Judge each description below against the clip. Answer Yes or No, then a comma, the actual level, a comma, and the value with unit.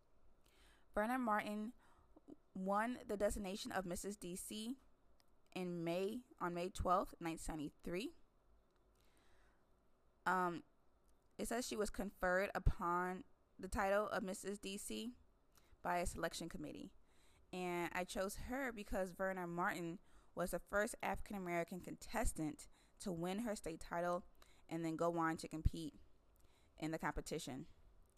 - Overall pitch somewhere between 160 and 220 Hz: Yes, medium, 185 Hz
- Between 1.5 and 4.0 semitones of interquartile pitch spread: Yes, average, 3.7 semitones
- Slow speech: Yes, slow, 120 wpm